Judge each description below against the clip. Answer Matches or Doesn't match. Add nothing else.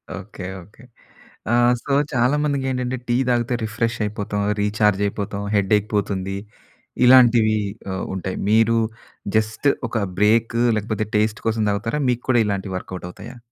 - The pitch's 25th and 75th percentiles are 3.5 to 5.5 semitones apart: Doesn't match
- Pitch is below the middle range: Matches